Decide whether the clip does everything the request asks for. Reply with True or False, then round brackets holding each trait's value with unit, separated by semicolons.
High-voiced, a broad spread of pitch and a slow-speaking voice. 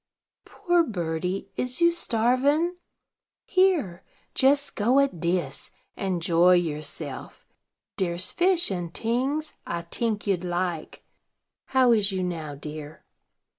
True (195 Hz; 7.9 semitones; 115 wpm)